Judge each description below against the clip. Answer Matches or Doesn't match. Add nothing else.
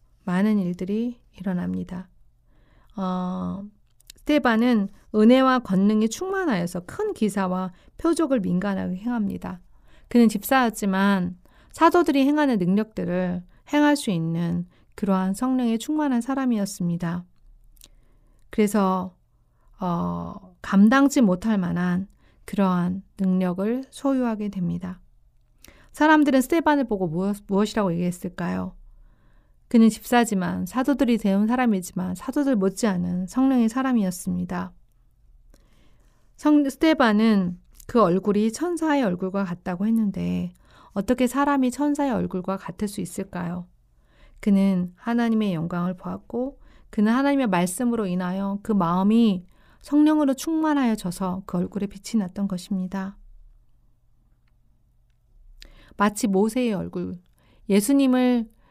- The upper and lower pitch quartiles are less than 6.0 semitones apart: Matches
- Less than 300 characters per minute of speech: Matches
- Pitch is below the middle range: Doesn't match